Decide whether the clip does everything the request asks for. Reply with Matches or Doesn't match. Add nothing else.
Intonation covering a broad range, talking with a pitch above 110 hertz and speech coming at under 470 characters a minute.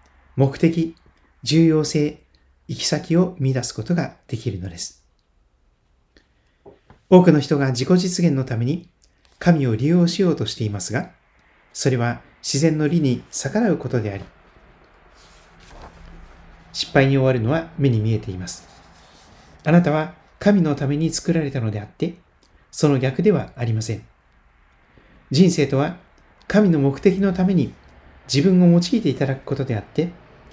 Matches